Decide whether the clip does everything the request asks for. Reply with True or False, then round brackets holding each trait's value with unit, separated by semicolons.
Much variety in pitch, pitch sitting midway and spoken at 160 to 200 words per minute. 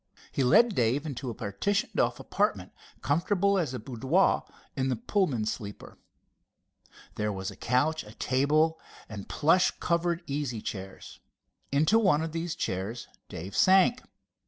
False (7.1 semitones; 145 Hz; 140 wpm)